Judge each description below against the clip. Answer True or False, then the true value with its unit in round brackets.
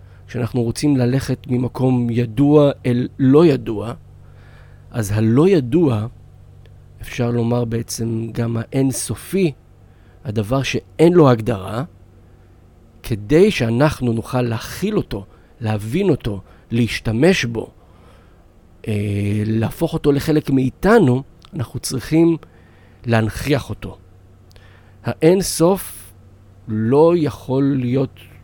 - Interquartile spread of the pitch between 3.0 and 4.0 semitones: False (5.0 semitones)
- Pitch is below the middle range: True (115 Hz)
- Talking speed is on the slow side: True (85 wpm)